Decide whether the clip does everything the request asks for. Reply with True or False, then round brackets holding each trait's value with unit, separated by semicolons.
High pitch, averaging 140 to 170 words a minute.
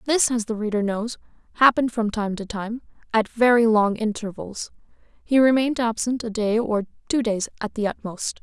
False (225 Hz; 180 wpm)